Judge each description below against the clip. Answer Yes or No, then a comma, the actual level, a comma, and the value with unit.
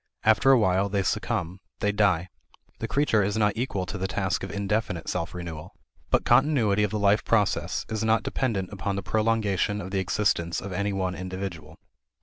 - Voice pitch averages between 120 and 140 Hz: No, low, 100 Hz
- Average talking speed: Yes, average, 185 wpm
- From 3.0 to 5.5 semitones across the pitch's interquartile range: No, narrow, 2.5 semitones